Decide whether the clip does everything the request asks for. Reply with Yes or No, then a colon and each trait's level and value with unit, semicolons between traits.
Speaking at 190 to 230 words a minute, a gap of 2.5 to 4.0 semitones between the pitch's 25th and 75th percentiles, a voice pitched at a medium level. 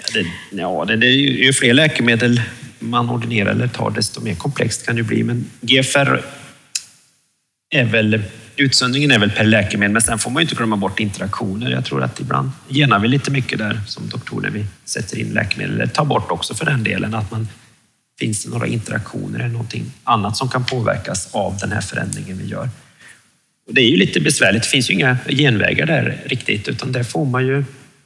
No: fast, 195 wpm; average, 3.1 semitones; low, 120 Hz